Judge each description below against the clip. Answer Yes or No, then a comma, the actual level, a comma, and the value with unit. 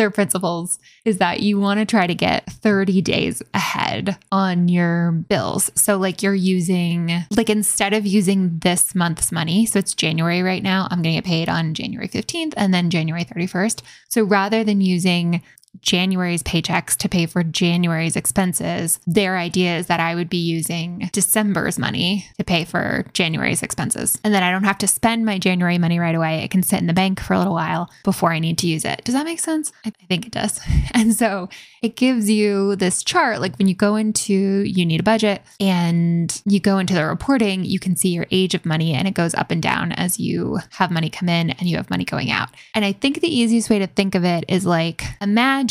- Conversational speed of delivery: No, fast, 220 wpm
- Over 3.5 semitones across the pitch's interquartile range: No, average, 3.2 semitones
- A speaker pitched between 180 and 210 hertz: Yes, medium, 185 Hz